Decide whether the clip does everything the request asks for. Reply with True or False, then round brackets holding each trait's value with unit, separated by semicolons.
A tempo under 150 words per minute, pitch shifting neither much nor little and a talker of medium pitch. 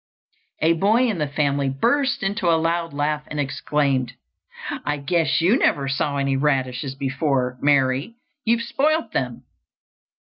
True (140 wpm; 4.4 semitones; 150 Hz)